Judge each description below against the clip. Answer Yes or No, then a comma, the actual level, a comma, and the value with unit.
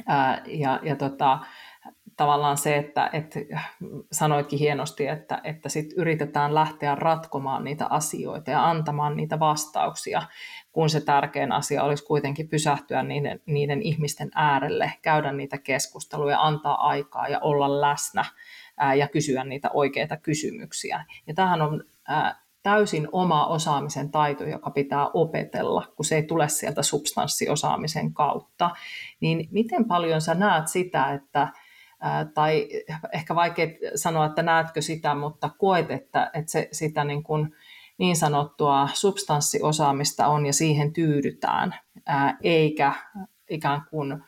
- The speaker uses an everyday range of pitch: No, narrow, 1.9 semitones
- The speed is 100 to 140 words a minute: Yes, average, 130 wpm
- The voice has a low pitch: No, medium, 150 Hz